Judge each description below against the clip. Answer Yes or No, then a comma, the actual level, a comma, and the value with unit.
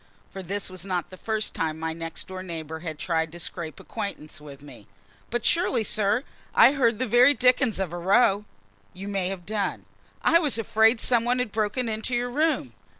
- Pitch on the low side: No, high, 205 Hz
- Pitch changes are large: Yes, wide, 5.7 semitones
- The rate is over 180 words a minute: Yes, average, 200 wpm